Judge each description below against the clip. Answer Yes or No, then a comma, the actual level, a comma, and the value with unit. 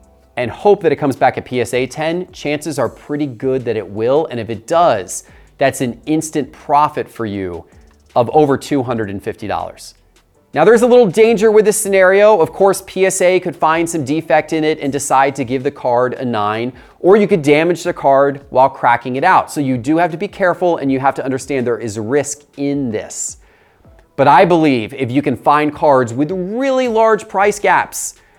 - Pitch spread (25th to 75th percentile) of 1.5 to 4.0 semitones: No, average, 5.2 semitones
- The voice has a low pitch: No, medium, 145 Hz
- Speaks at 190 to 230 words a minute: Yes, average, 200 wpm